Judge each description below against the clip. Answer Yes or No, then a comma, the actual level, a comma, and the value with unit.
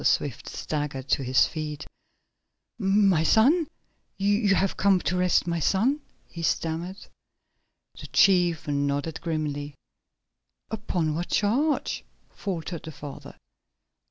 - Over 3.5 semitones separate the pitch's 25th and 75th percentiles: Yes, average, 4.6 semitones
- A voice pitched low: No, medium, 170 Hz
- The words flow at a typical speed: No, slow, 110 wpm